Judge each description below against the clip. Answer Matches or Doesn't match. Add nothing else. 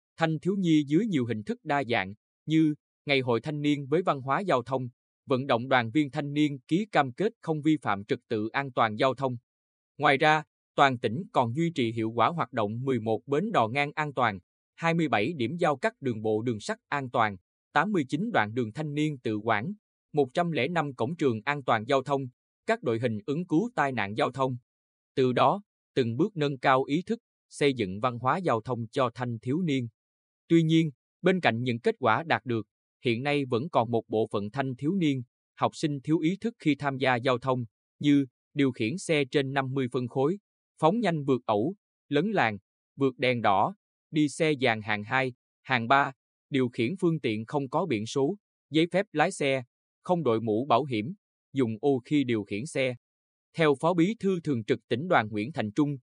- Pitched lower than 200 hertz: Matches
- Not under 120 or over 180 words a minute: Doesn't match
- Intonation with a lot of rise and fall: Doesn't match